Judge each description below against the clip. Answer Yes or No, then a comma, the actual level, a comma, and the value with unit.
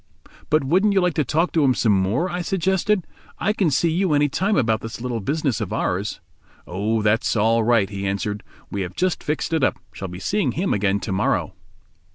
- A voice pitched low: Yes, low, 130 Hz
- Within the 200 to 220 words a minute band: Yes, fast, 205 wpm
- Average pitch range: No, wide, 8.8 semitones